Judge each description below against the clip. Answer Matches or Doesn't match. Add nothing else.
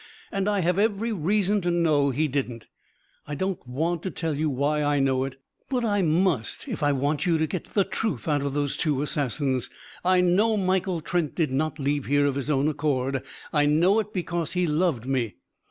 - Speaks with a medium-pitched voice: Matches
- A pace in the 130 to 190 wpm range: Doesn't match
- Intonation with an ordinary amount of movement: Matches